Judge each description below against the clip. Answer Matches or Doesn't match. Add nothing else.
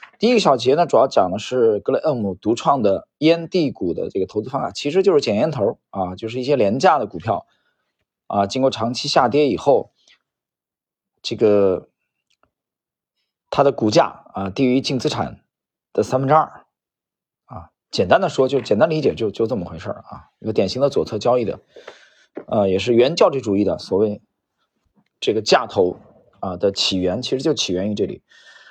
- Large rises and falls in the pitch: Matches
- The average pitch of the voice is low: Matches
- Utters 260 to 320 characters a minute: Matches